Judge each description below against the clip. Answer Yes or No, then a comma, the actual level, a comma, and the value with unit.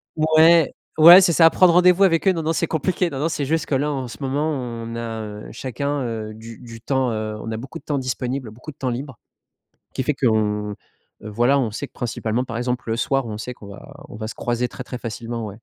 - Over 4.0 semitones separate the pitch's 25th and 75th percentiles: Yes, average, 4.7 semitones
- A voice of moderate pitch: No, low, 125 Hz